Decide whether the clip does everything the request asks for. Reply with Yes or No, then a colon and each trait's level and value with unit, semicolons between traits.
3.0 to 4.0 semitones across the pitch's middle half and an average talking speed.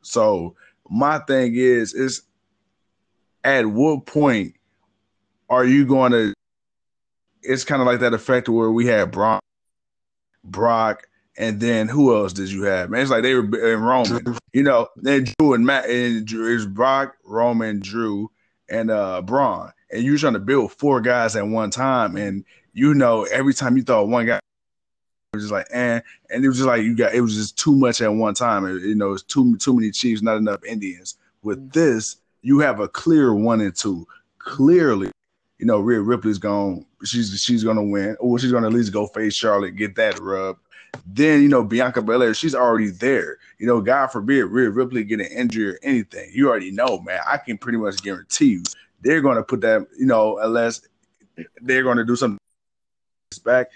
Yes: average, 3.6 semitones; average, 195 wpm